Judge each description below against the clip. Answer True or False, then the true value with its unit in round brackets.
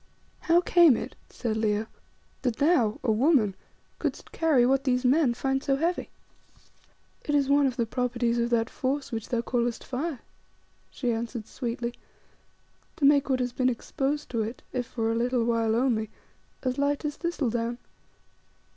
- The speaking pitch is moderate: False (250 Hz)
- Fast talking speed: False (165 wpm)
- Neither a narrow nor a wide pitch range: True (3.2 semitones)